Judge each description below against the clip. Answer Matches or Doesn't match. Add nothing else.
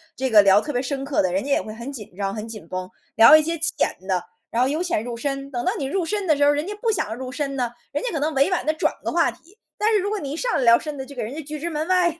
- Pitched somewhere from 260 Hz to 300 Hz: Matches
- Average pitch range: Doesn't match